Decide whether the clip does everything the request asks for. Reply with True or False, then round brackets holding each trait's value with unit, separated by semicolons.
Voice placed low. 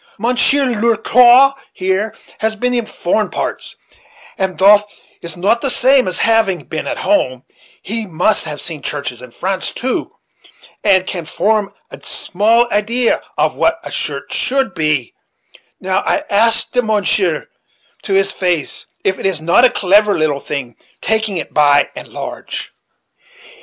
False (205 Hz)